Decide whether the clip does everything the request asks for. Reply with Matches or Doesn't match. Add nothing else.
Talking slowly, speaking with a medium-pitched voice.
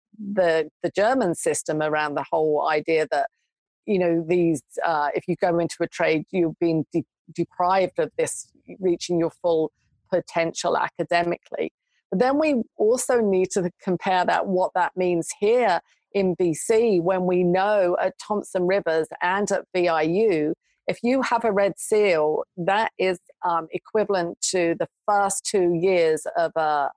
Doesn't match